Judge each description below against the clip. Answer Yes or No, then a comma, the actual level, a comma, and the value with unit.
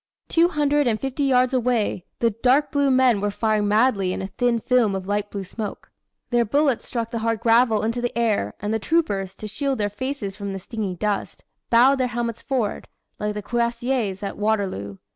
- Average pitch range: Yes, average, 3.5 semitones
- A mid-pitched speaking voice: No, high, 230 Hz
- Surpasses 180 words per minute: Yes, average, 200 wpm